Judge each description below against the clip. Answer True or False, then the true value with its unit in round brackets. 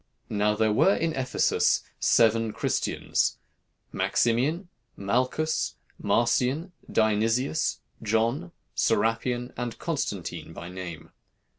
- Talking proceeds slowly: True (90 wpm)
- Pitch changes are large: False (3.4 semitones)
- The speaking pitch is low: True (115 Hz)